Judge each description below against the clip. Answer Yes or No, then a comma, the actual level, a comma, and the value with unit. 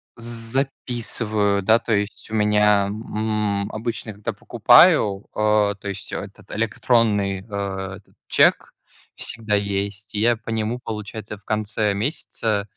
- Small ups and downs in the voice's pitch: Yes, narrow, 1.7 semitones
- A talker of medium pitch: No, low, 105 Hz